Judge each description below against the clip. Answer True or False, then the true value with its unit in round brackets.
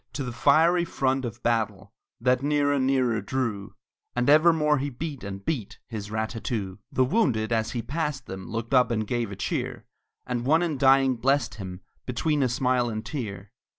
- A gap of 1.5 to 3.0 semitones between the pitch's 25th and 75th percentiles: False (4.1 semitones)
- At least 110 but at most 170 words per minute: False (185 wpm)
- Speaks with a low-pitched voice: True (125 Hz)